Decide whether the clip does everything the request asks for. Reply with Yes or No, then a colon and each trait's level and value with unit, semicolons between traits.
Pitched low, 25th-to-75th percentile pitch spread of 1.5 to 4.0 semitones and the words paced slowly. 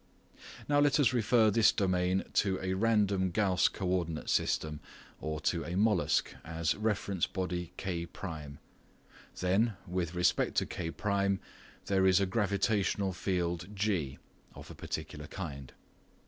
Yes: very low, 95 Hz; average, 2.9 semitones; slow, 130 wpm